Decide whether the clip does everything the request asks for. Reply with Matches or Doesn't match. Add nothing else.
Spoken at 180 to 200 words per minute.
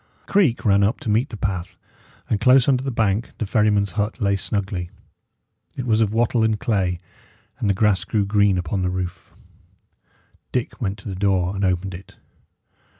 Matches